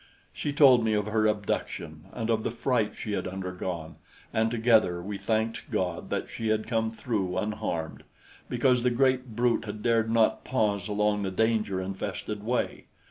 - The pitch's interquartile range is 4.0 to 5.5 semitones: No, narrow, 2.6 semitones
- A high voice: No, low, 110 Hz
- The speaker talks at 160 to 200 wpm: Yes, average, 170 wpm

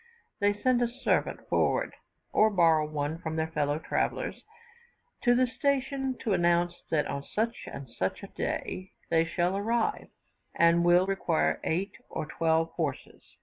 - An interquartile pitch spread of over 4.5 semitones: Yes, wide, 5.6 semitones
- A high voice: No, medium, 175 Hz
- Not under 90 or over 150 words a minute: Yes, average, 145 wpm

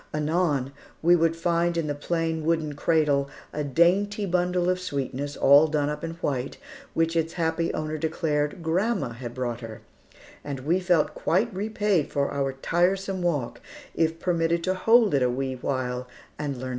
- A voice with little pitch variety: No, average, 3.7 semitones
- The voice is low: No, medium, 160 Hz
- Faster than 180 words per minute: No, average, 175 wpm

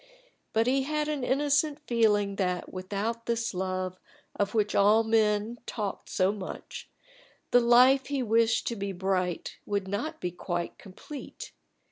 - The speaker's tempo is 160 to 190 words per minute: No, average, 145 wpm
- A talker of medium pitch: No, high, 215 Hz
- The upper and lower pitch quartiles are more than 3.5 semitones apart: Yes, average, 4.1 semitones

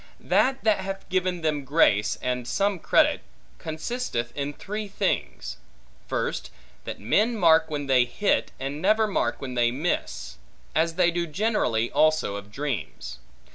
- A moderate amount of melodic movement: No, wide, 7.5 semitones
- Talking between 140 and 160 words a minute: Yes, average, 145 wpm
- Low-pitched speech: No, medium, 155 Hz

